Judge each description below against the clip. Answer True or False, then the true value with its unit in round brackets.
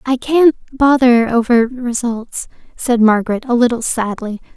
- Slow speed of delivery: True (130 wpm)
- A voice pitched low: False (240 Hz)